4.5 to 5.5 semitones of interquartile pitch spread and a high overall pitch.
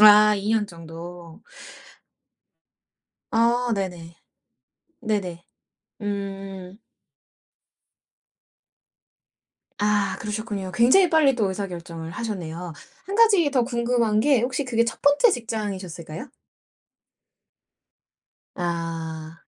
Yes: average, 5.2 semitones; high, 205 Hz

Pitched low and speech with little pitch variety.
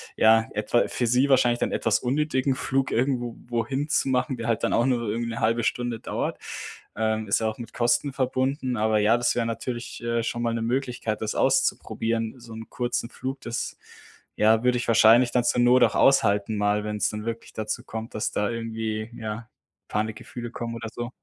Yes: low, 115 Hz; narrow, 1.9 semitones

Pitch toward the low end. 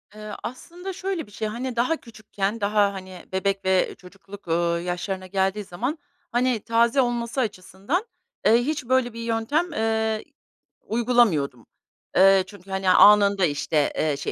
No: high, 210 Hz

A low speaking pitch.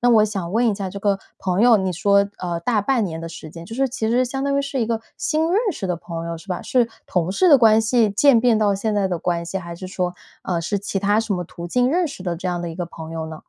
No: high, 200 Hz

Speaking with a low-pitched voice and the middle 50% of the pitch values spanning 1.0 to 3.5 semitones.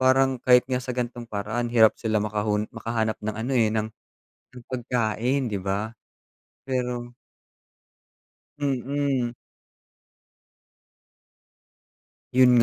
Yes: low, 120 Hz; narrow, 2.5 semitones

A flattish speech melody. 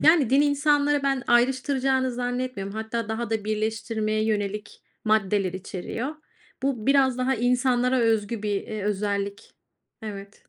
No: average, 3.8 semitones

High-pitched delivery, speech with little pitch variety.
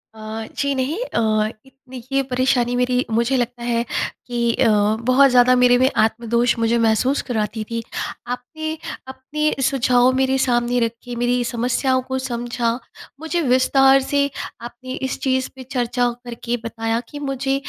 Yes: very high, 250 Hz; narrow, 1.9 semitones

